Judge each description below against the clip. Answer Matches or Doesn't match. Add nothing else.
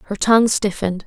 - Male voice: Doesn't match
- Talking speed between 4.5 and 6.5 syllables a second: Doesn't match